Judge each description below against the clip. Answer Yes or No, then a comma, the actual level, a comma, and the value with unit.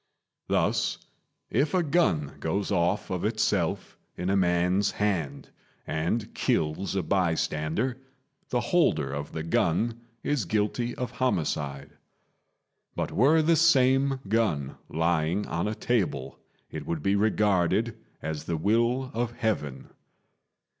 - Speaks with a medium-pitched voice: No, low, 100 Hz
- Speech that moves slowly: Yes, slow, 125 wpm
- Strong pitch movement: Yes, wide, 6.5 semitones